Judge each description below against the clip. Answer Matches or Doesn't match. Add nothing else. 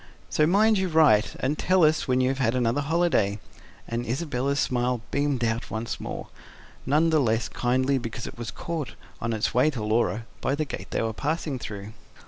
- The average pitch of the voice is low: Matches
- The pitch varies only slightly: Doesn't match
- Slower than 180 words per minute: Doesn't match